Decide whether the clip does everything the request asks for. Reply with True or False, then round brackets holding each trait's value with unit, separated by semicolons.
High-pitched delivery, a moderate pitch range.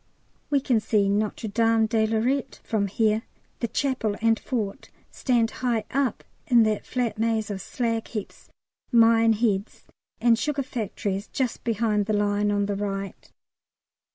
False (225 Hz; 2.3 semitones)